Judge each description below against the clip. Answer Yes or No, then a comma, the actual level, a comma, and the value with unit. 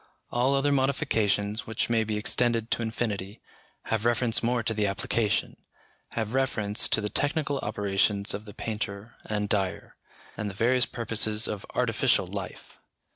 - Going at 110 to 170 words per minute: Yes, average, 150 wpm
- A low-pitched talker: Yes, low, 110 Hz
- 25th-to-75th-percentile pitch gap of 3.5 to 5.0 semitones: No, narrow, 2.6 semitones